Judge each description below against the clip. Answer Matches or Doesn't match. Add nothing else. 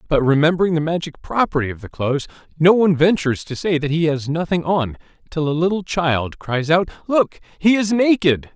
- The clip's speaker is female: Doesn't match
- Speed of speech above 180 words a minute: Matches